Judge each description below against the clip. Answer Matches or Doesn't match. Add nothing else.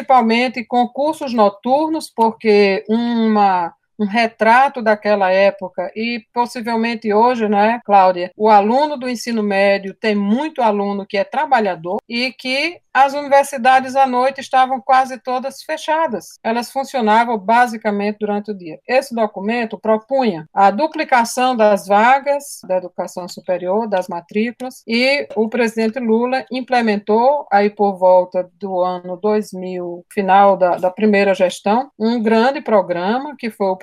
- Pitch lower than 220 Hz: Doesn't match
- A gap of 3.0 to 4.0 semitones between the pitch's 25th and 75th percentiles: Doesn't match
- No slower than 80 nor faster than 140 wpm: Matches